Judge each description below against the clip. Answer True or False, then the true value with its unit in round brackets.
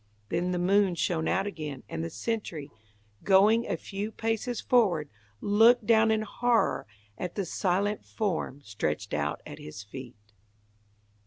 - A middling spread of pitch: False (7.5 semitones)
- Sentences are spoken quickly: False (145 wpm)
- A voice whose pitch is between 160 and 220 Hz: True (190 Hz)